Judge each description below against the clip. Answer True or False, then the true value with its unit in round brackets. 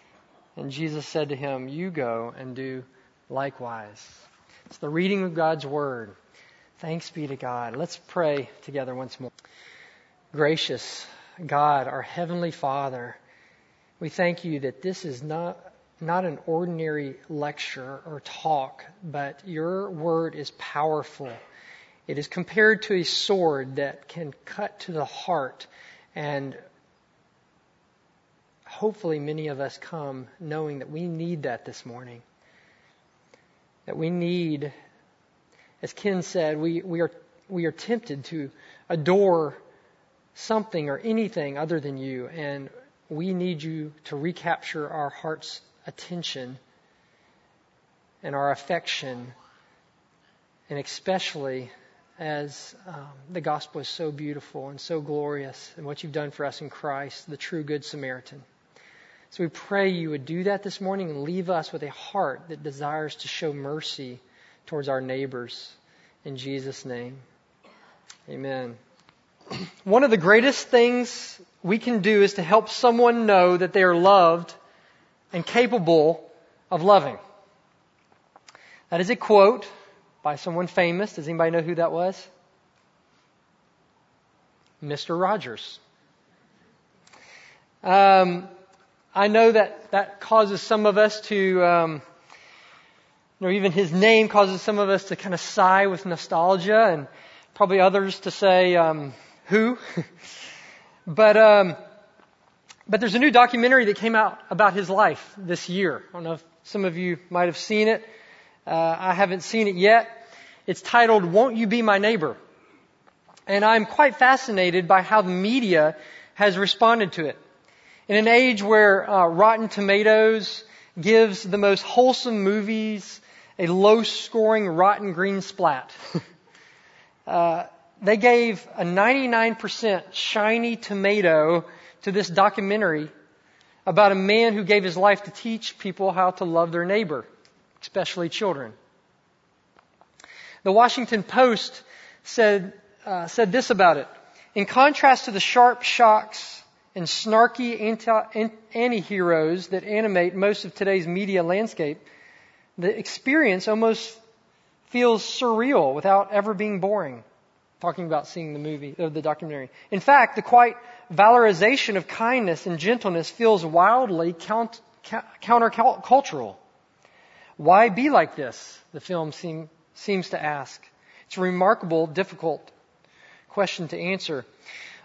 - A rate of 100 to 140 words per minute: True (135 wpm)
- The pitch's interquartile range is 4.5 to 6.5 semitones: True (5.3 semitones)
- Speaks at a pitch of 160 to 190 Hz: True (185 Hz)